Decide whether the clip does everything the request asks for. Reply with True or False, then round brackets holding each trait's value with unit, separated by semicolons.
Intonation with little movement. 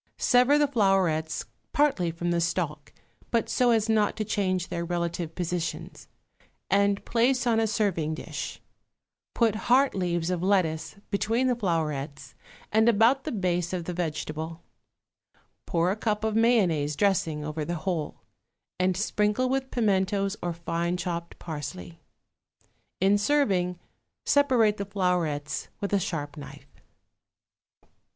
False (4.6 semitones)